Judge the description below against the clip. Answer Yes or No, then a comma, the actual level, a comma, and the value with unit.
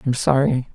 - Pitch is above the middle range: No, low, 130 Hz